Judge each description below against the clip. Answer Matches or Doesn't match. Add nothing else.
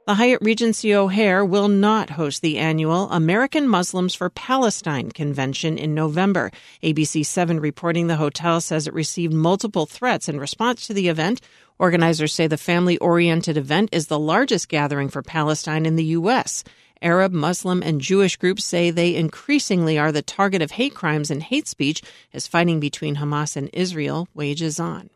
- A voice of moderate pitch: Matches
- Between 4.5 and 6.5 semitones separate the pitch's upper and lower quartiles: Doesn't match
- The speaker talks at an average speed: Matches